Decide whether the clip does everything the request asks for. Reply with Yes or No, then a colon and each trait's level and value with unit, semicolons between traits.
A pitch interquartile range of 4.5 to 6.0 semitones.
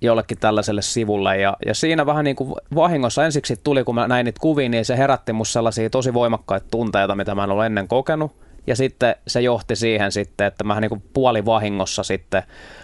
No: average, 3.7 semitones